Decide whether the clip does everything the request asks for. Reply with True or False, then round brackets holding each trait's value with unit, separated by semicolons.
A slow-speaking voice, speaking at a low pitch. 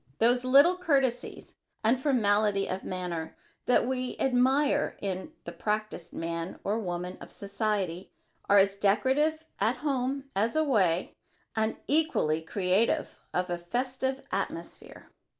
False (125 wpm; 220 Hz)